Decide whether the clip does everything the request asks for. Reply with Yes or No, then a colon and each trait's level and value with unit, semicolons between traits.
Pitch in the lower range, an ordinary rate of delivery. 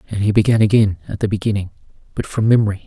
No: low, 105 Hz; fast, 210 wpm